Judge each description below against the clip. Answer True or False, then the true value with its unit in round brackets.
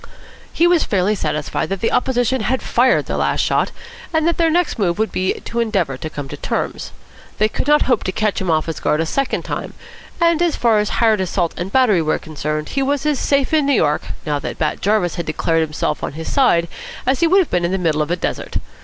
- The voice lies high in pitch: True (210 Hz)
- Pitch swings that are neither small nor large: False (8.4 semitones)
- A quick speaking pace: True (240 wpm)